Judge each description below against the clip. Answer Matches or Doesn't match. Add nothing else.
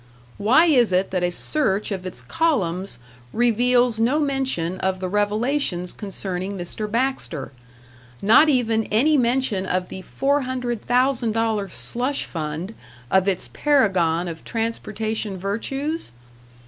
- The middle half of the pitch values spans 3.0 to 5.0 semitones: Doesn't match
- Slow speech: Matches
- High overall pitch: Matches